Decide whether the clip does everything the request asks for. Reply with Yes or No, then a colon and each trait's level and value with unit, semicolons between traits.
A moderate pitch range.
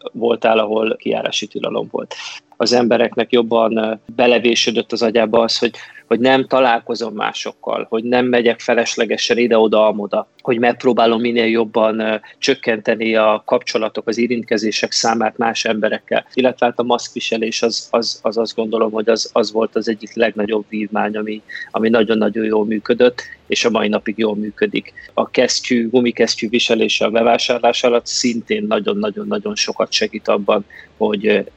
No: narrow, 1.6 semitones